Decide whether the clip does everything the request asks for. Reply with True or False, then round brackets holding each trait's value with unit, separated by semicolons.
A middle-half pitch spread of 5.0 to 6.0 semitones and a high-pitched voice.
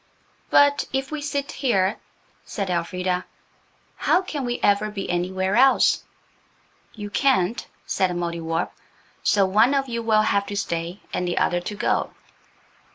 True (5.6 semitones; 205 Hz)